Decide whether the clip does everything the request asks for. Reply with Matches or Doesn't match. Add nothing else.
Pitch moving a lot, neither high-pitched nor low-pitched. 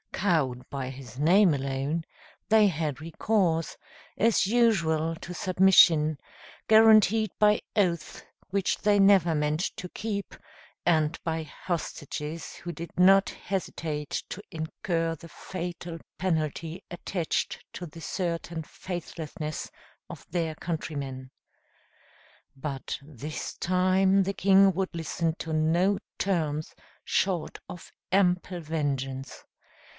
Doesn't match